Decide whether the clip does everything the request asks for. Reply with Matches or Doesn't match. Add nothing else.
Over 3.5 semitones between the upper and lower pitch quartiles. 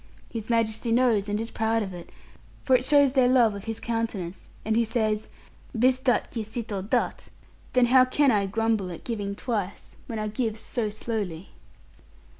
Doesn't match